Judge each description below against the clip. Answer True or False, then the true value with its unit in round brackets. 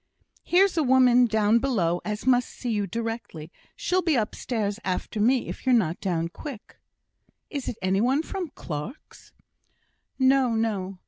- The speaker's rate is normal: True (150 wpm)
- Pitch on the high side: True (230 Hz)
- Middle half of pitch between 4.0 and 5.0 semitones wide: True (4.7 semitones)